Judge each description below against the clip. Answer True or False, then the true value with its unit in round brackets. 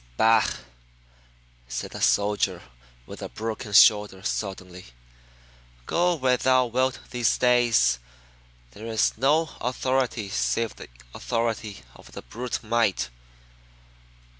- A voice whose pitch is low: True (115 Hz)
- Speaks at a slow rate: True (105 wpm)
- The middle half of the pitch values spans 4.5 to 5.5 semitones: False (3.4 semitones)